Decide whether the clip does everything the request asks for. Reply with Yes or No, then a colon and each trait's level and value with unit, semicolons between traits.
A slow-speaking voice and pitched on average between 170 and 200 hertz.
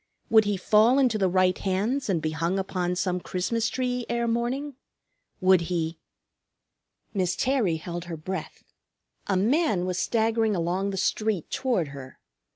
No: average, 155 wpm; high, 190 Hz